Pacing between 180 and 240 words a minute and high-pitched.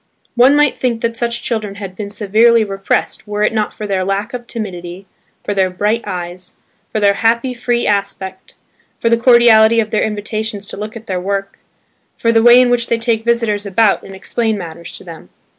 Yes: average, 200 wpm; high, 215 Hz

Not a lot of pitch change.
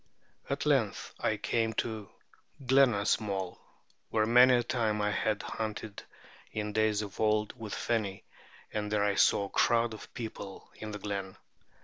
Yes: narrow, 1.8 semitones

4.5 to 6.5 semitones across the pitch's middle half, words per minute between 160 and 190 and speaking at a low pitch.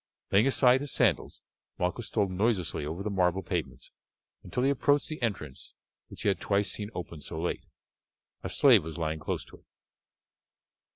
Yes: wide, 5.6 semitones; average, 170 wpm; low, 100 Hz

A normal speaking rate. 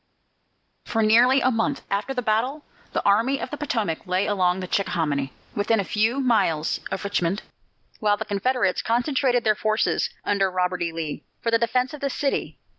Yes: average, 180 wpm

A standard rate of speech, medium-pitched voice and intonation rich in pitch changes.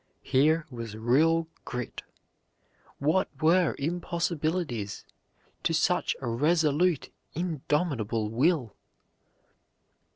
No: slow, 75 wpm; medium, 150 Hz; wide, 5.7 semitones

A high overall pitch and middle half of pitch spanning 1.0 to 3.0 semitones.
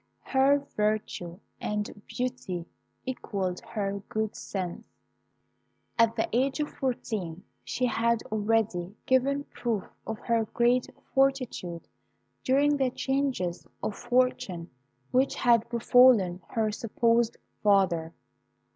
No: high, 230 Hz; average, 4.4 semitones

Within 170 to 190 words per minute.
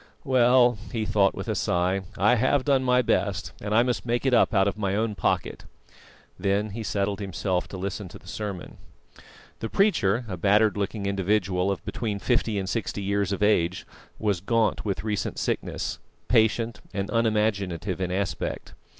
Yes: average, 175 wpm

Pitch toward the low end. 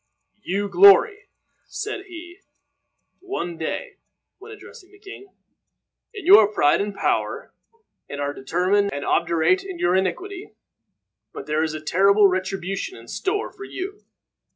No: high, 205 Hz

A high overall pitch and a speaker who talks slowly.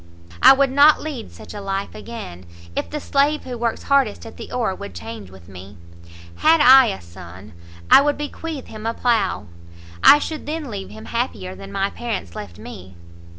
No: high, 225 Hz; average, 190 wpm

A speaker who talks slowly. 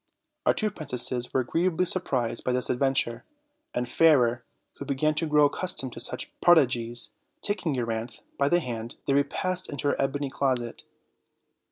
No: average, 160 wpm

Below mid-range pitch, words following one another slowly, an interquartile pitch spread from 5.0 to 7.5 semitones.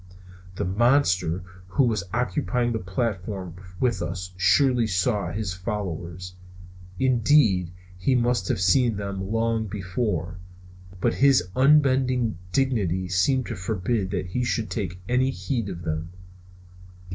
Yes: low, 105 Hz; slow, 125 wpm; average, 5.3 semitones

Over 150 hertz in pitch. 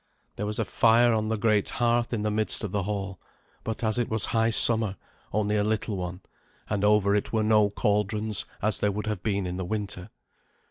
No: low, 105 Hz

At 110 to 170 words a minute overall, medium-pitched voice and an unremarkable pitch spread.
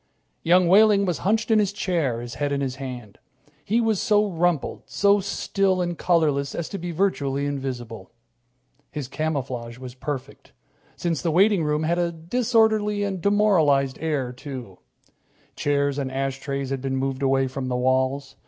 No: average, 160 wpm; medium, 150 Hz; wide, 5.8 semitones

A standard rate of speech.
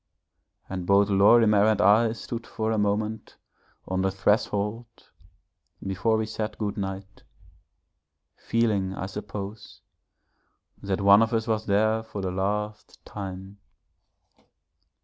No: slow, 120 wpm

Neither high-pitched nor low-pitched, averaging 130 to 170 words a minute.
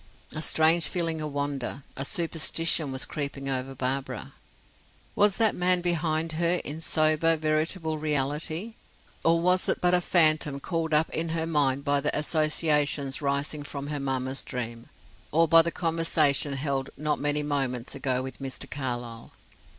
Yes: medium, 150 Hz; average, 155 wpm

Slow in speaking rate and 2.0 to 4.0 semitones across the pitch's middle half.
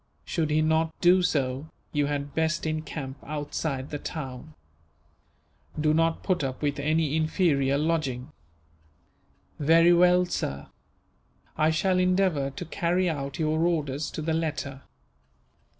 Yes: slow, 130 wpm; average, 2.7 semitones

